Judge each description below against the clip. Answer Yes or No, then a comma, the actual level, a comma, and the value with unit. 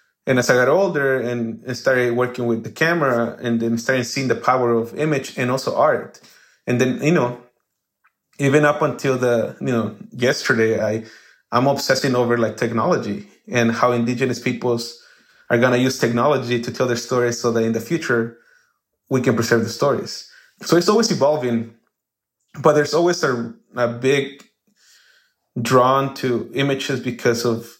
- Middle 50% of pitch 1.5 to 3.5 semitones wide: Yes, narrow, 2.5 semitones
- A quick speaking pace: No, average, 165 wpm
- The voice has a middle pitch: No, low, 125 Hz